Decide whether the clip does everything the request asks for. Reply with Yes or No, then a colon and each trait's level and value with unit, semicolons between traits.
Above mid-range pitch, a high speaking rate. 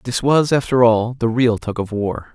No: low, 120 Hz; fast, 230 wpm